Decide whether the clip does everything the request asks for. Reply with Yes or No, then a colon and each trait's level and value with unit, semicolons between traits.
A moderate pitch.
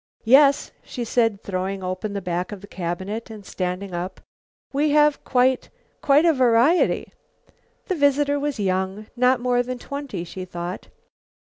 No: high, 225 Hz